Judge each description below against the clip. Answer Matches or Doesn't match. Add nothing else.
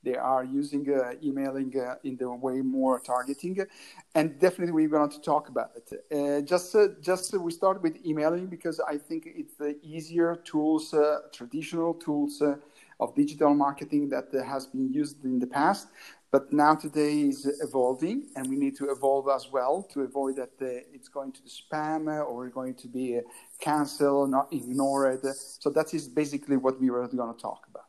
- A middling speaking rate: Doesn't match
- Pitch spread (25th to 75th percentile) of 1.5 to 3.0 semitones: Matches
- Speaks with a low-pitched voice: Doesn't match